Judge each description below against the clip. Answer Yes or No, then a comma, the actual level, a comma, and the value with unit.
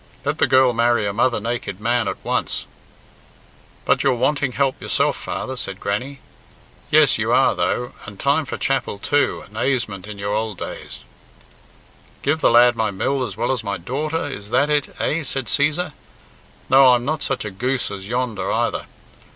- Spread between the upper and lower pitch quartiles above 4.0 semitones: Yes, average, 4.4 semitones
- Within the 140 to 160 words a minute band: No, average, 185 wpm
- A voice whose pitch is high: No, low, 125 Hz